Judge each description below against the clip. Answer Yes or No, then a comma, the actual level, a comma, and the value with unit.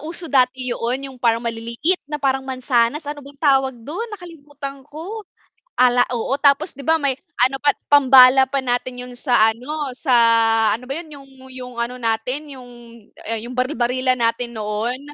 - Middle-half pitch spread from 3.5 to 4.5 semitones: No, average, 2.7 semitones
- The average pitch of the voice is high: Yes, very high, 260 Hz